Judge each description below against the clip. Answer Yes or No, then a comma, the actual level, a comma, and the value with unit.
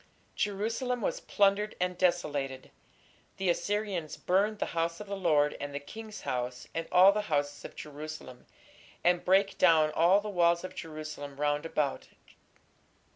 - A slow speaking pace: No, average, 150 wpm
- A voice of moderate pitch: Yes, medium, 170 Hz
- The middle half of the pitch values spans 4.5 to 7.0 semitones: Yes, average, 5.0 semitones